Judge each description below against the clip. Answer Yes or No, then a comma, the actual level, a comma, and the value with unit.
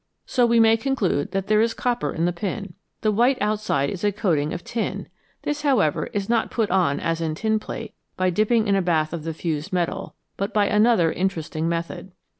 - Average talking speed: No, fast, 210 wpm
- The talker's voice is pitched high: Yes, high, 195 Hz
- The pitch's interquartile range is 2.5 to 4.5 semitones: No, average, 4.9 semitones